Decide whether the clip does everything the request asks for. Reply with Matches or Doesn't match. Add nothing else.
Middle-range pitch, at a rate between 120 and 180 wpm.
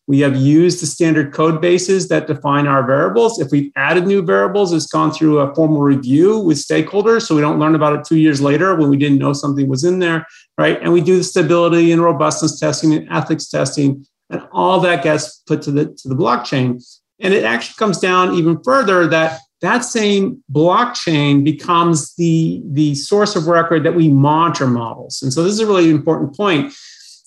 Doesn't match